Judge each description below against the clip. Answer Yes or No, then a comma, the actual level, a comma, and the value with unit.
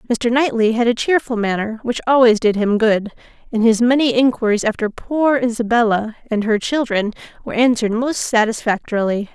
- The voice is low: No, high, 230 Hz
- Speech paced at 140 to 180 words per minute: Yes, average, 160 wpm